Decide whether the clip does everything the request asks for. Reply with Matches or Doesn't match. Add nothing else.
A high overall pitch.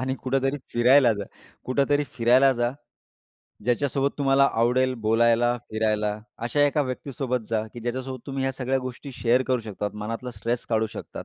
Doesn't match